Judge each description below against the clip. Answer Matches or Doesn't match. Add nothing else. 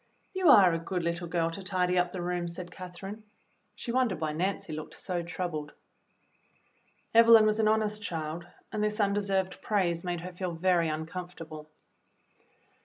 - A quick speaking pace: Doesn't match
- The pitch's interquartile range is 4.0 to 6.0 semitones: Doesn't match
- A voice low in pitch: Doesn't match